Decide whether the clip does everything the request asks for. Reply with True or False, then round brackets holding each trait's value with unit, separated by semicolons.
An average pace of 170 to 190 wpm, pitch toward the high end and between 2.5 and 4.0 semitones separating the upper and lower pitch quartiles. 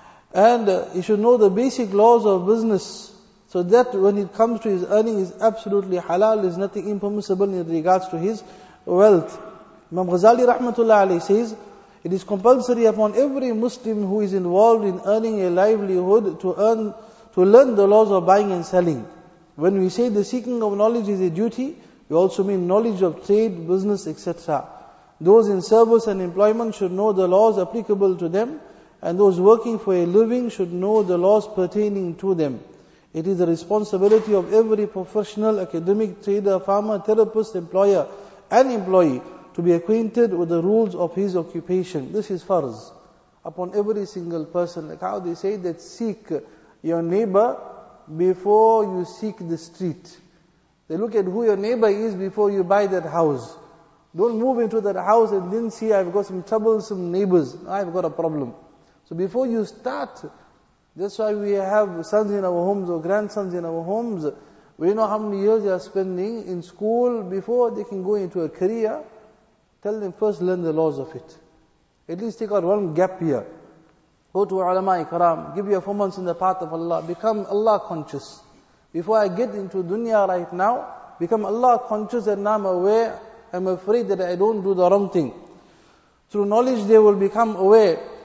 True (180 wpm; 200 Hz; 3.2 semitones)